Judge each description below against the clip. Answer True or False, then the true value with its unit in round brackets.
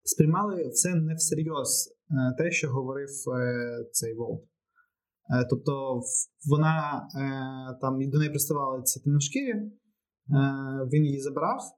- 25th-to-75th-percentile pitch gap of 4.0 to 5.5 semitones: False (3.3 semitones)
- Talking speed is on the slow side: True (100 wpm)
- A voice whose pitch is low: False (145 Hz)